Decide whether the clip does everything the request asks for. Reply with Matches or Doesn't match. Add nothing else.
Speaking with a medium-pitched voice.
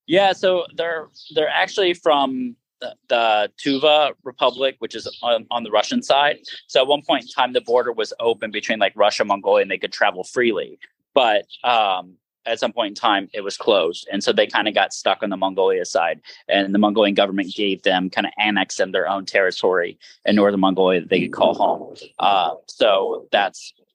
Matches